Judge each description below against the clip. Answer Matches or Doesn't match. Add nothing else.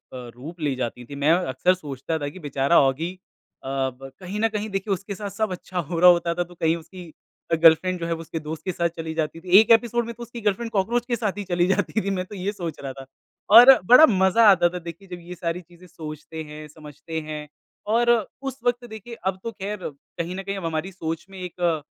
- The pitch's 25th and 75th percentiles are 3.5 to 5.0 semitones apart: Matches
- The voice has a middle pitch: Matches